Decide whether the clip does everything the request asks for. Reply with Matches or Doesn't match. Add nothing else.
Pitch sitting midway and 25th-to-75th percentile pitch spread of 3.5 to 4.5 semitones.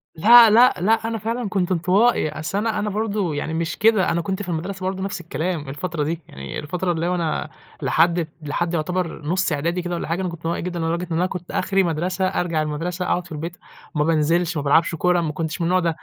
Doesn't match